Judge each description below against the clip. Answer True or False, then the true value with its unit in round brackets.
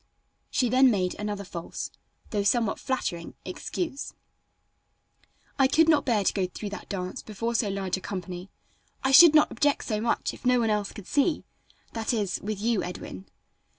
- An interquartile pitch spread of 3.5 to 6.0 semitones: True (5.0 semitones)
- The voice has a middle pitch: False (215 Hz)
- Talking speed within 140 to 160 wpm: False (175 wpm)